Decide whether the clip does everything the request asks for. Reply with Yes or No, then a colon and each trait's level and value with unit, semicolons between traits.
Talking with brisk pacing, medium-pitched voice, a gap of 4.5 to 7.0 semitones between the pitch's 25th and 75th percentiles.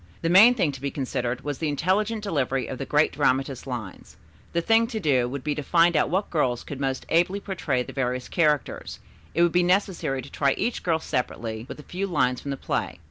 Yes: fast, 225 wpm; medium, 150 Hz; average, 5.2 semitones